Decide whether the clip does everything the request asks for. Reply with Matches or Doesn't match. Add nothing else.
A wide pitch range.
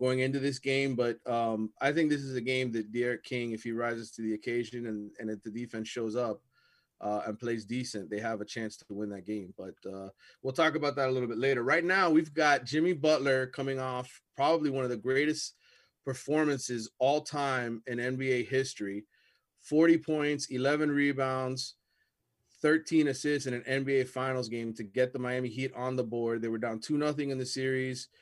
Doesn't match